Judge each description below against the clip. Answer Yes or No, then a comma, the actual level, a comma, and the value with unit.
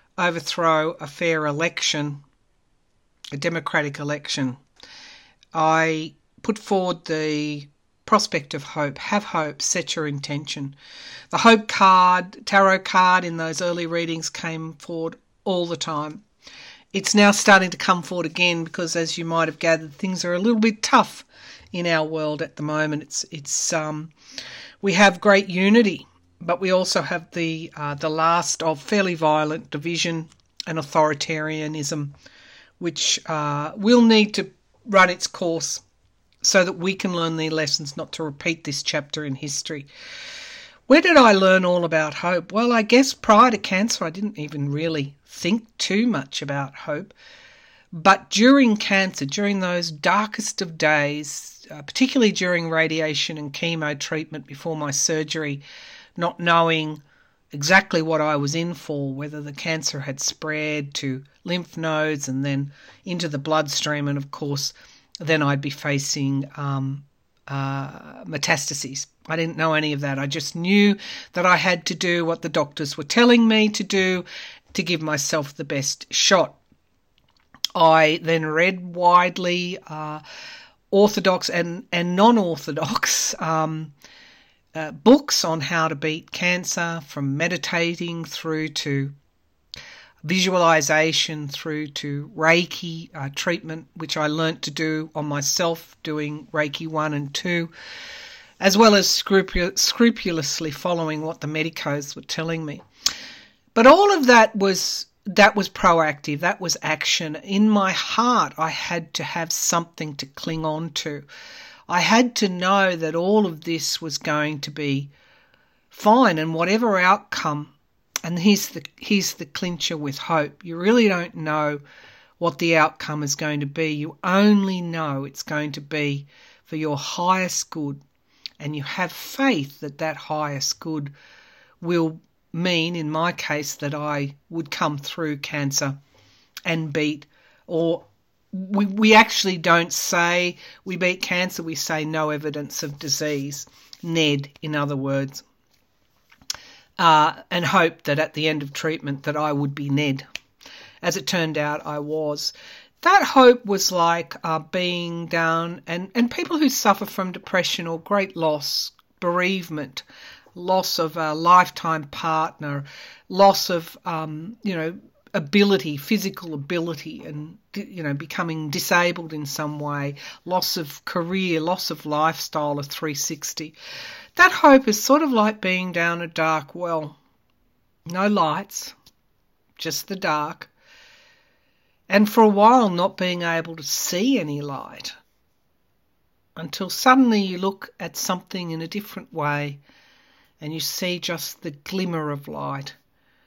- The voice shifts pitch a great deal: No, average, 3.8 semitones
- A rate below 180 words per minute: Yes, average, 145 wpm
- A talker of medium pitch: Yes, medium, 165 Hz